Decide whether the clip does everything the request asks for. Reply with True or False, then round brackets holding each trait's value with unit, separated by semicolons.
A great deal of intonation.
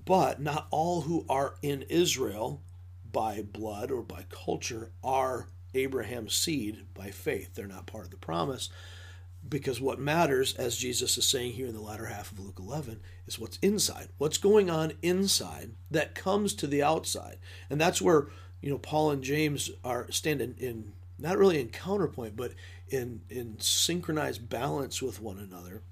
True (7.5 semitones)